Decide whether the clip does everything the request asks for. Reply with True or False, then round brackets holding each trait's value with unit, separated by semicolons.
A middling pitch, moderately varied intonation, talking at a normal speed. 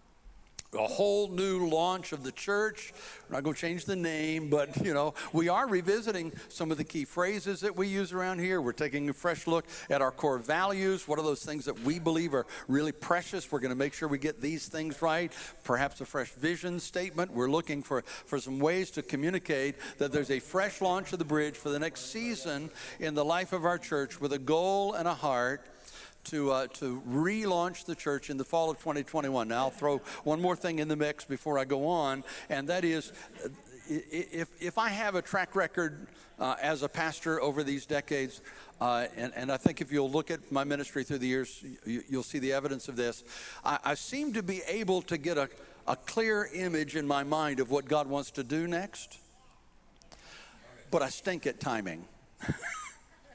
False (155 Hz; 4.1 semitones; 210 wpm)